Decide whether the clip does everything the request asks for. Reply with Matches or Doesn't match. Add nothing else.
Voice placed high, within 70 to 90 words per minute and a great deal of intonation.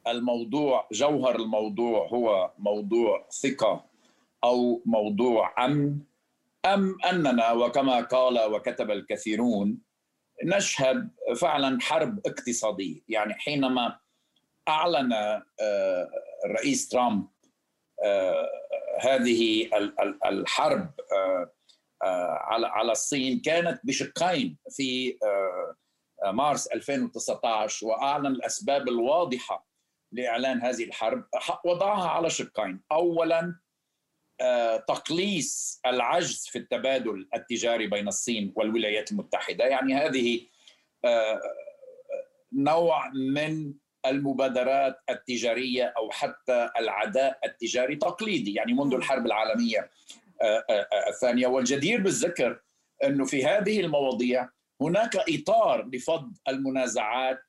Doesn't match